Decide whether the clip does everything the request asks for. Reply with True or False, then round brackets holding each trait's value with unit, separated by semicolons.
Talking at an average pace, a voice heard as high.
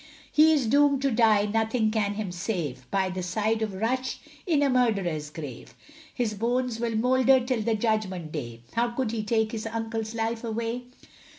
True (180 wpm; 225 Hz)